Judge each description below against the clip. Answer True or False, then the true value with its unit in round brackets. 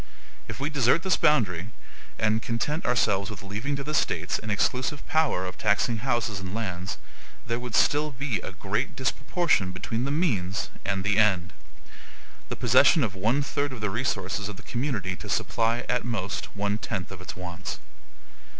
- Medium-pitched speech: False (110 Hz)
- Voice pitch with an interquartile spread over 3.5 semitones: True (5.2 semitones)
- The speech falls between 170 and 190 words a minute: True (175 wpm)